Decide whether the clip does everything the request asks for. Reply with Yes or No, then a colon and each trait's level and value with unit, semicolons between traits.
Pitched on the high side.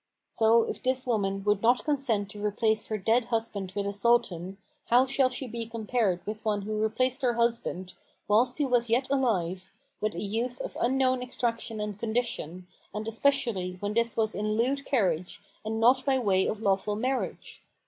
Yes: high, 225 Hz